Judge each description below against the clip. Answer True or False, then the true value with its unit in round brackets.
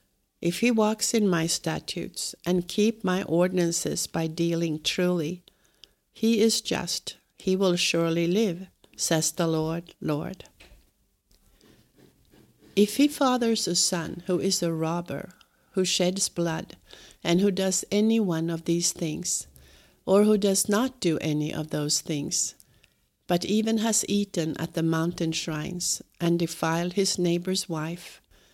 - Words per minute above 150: False (140 wpm)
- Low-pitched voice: False (175 Hz)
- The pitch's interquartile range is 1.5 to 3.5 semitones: True (3.0 semitones)